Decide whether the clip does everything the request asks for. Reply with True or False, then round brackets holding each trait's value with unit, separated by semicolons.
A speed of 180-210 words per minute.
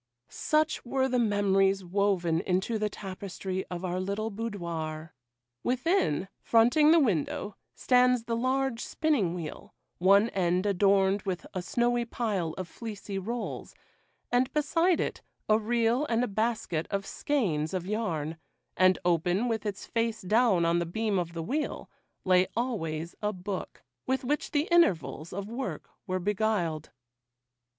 False (140 wpm)